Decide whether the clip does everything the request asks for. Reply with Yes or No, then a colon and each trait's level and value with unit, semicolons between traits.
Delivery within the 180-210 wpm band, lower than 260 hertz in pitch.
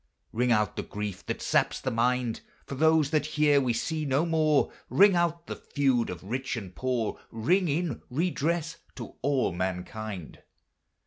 No: average, 165 wpm; low, 135 Hz